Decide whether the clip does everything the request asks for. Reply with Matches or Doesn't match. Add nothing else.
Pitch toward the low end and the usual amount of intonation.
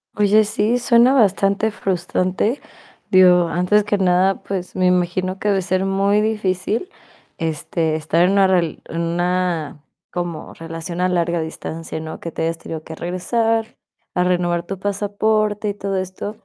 Doesn't match